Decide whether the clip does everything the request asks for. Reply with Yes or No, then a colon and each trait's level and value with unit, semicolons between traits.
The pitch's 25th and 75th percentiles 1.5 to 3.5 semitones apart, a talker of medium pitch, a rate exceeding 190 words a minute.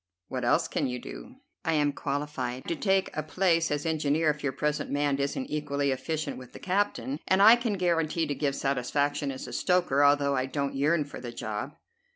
Yes: average, 3.1 semitones; medium, 145 Hz; average, 200 wpm